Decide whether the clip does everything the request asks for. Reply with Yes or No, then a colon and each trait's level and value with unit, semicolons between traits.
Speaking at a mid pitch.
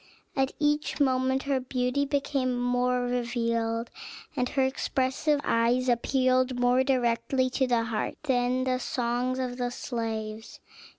No: very high, 250 Hz